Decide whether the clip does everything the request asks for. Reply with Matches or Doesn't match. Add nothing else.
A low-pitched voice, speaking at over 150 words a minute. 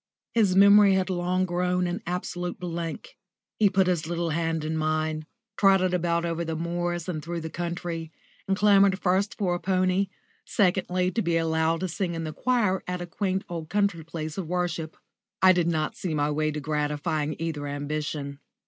Doesn't match